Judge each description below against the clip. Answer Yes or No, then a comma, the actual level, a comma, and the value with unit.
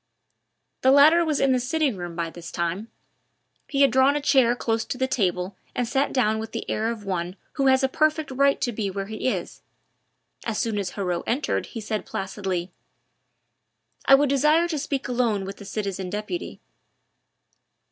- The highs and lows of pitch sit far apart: Yes, wide, 5.7 semitones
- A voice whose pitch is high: Yes, high, 230 Hz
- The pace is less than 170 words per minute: No, average, 185 wpm